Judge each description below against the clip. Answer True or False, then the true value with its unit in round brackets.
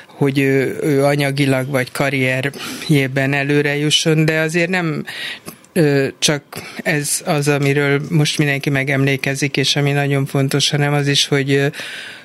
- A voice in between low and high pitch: True (145 Hz)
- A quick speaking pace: False (130 wpm)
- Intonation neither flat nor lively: False (1.5 semitones)